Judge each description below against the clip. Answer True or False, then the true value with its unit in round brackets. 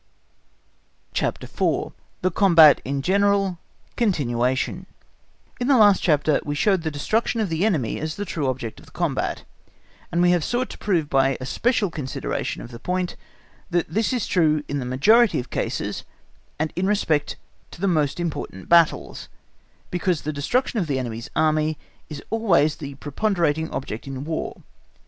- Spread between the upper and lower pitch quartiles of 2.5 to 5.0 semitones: False (5.5 semitones)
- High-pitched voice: False (160 Hz)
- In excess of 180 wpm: False (165 wpm)